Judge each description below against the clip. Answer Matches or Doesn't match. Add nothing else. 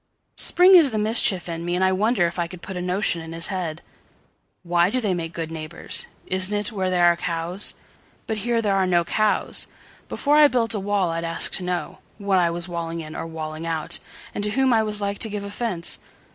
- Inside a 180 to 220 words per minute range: Matches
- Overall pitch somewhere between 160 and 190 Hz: Matches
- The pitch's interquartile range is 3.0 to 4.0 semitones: Matches